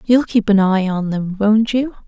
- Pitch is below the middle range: No, high, 210 Hz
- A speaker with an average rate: No, fast, 230 wpm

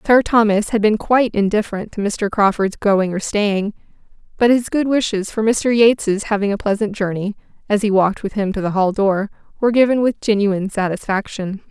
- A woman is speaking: Yes, female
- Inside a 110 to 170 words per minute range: No, average, 190 wpm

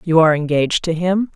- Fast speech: Yes, fast, 220 wpm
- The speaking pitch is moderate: Yes, medium, 170 Hz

